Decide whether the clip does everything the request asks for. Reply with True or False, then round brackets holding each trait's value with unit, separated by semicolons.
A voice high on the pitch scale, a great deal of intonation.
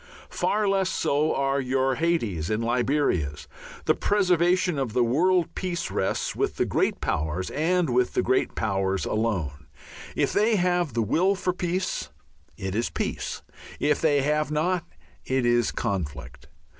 False (135 Hz; 8.3 semitones)